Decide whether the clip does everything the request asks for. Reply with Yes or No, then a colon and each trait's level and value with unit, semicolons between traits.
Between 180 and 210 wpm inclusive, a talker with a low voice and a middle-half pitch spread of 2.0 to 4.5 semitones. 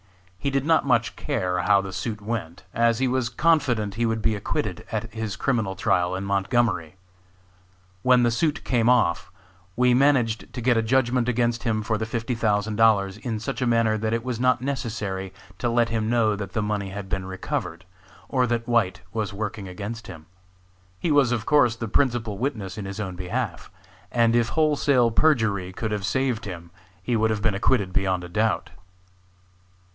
Yes: average, 190 wpm; low, 110 Hz; average, 3.4 semitones